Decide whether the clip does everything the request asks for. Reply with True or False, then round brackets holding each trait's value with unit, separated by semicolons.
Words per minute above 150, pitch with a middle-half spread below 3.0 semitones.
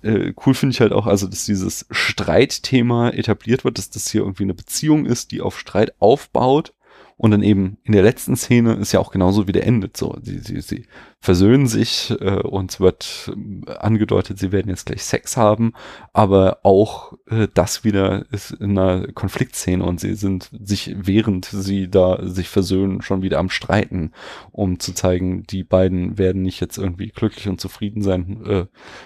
True (180 wpm; 2.6 semitones)